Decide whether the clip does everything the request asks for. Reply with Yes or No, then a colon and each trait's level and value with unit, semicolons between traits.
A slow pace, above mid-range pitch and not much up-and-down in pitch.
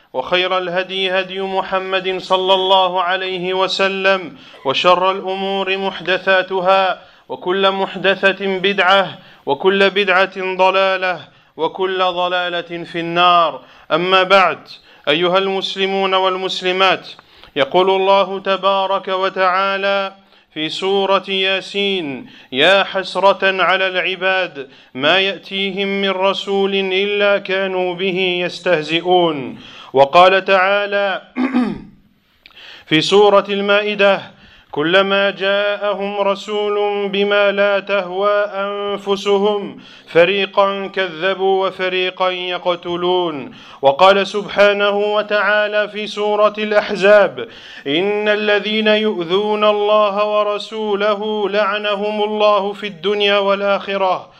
Yes: slow, 85 wpm; high, 195 Hz; narrow, 1.3 semitones